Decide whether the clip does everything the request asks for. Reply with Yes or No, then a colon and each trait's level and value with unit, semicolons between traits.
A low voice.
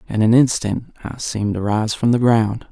Yes: low, 110 Hz